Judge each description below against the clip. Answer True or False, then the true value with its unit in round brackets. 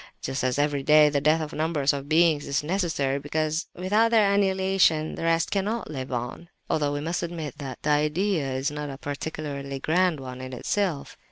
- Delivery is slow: False (185 wpm)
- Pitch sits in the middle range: True (150 Hz)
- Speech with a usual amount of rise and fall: True (3.5 semitones)